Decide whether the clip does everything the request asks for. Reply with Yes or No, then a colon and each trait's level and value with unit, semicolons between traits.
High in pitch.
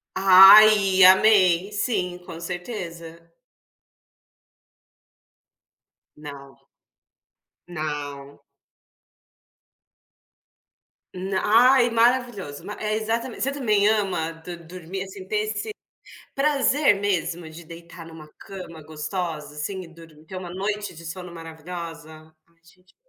No: medium, 180 Hz